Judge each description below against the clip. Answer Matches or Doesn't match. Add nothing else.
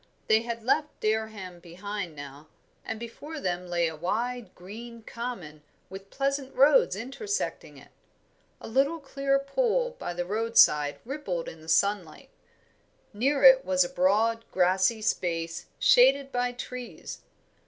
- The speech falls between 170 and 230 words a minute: Doesn't match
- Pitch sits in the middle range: Doesn't match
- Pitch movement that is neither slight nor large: Doesn't match